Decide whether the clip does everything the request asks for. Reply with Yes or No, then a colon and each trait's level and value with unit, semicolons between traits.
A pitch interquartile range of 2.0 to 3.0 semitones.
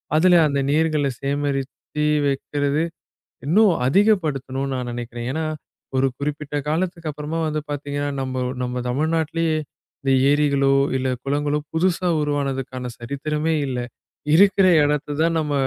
Yes: average, 2.7 semitones